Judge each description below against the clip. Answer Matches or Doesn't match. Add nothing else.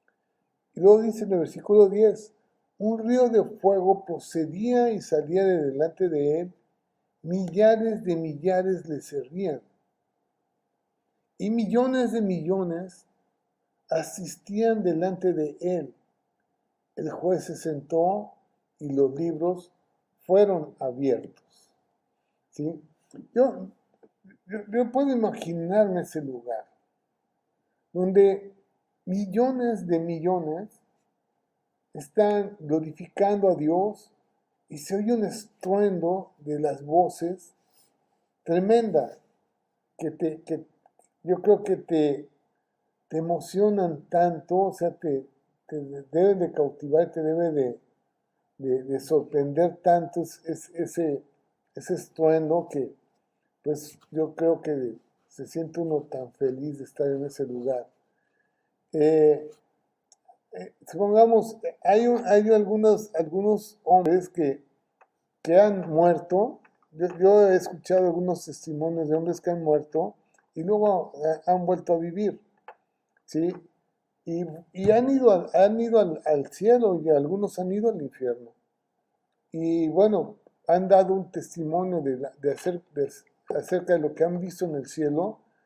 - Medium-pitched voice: Matches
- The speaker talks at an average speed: Doesn't match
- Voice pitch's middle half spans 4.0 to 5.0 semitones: Matches